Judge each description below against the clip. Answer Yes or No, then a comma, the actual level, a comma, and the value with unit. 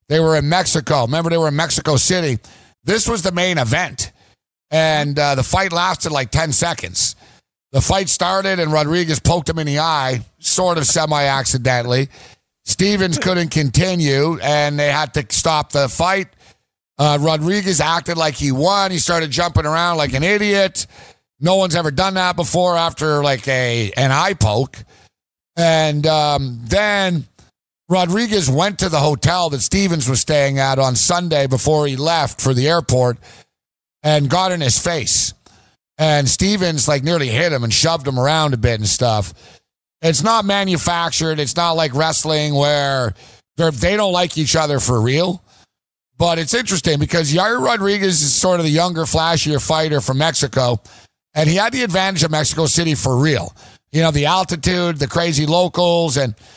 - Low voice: No, medium, 155 Hz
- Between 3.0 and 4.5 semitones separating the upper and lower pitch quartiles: Yes, average, 4.1 semitones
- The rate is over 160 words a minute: Yes, average, 170 wpm